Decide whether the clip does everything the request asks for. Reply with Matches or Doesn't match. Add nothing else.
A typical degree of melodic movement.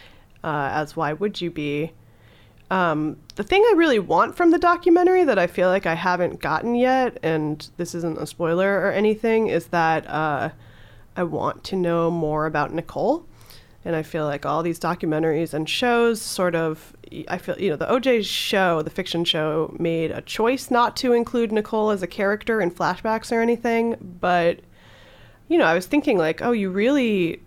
Doesn't match